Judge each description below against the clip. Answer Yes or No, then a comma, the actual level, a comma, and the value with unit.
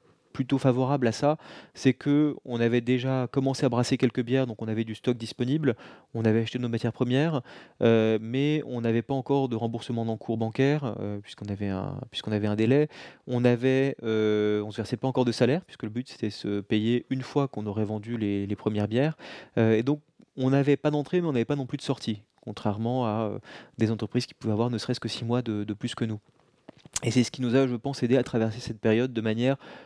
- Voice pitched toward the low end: Yes, low, 120 Hz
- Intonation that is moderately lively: Yes, average, 3.2 semitones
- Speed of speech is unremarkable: No, fast, 235 wpm